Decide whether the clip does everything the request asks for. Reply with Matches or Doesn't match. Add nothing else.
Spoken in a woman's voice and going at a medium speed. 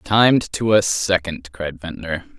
Doesn't match